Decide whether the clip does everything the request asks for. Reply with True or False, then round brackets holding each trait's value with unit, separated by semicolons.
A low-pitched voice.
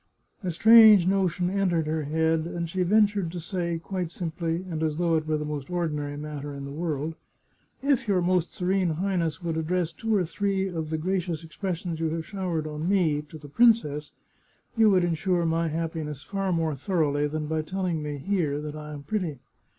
False (165 Hz)